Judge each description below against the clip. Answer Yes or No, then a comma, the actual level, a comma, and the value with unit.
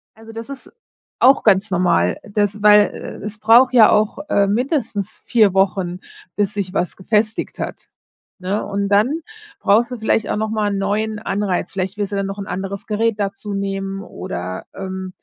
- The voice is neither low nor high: No, high, 205 Hz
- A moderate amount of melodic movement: No, narrow, 1.9 semitones